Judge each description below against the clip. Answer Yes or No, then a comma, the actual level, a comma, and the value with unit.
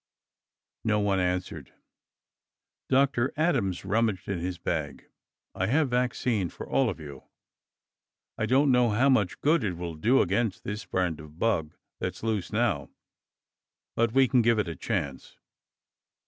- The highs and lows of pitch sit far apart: Yes, wide, 5.8 semitones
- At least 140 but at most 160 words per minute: Yes, average, 145 wpm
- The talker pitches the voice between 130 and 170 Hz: No, low, 105 Hz